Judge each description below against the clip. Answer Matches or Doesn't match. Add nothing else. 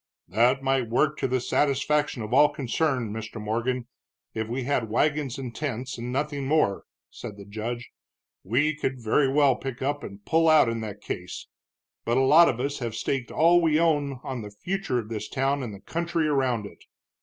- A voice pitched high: Doesn't match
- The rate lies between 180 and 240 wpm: Matches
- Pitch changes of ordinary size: Matches